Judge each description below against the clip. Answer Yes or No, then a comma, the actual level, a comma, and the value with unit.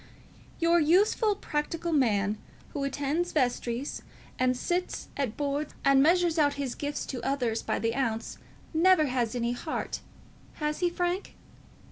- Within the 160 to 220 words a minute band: No, average, 140 wpm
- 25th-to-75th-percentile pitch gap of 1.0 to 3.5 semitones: No, average, 5.0 semitones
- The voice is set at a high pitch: Yes, very high, 285 Hz